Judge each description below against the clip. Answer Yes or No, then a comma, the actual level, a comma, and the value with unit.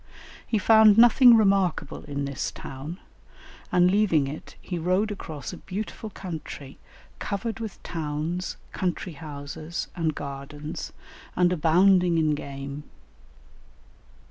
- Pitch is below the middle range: No, medium, 170 Hz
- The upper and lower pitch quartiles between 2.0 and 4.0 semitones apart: No, average, 5.0 semitones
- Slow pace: Yes, slow, 115 wpm